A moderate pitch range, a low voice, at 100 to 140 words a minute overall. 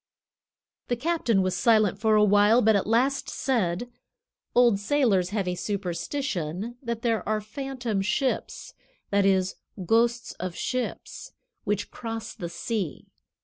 No: average, 3.8 semitones; high, 215 Hz; slow, 135 wpm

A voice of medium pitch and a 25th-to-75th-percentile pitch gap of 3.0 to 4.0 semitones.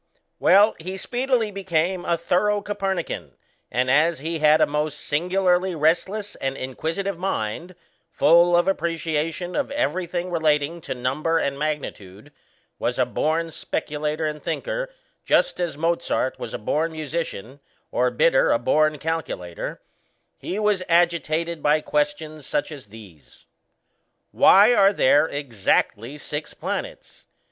Yes: medium, 160 Hz; average, 3.6 semitones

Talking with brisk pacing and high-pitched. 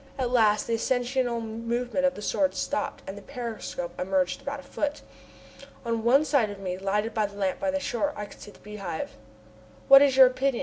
Yes: fast, 210 wpm; high, 235 Hz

